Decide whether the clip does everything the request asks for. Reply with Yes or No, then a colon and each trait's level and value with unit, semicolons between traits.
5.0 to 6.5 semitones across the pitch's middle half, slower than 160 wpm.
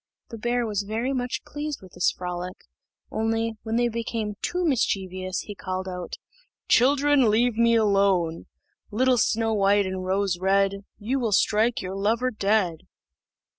No: average, 3.6 semitones; average, 150 wpm